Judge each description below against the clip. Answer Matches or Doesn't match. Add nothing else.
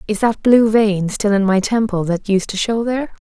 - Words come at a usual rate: Doesn't match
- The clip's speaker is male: Doesn't match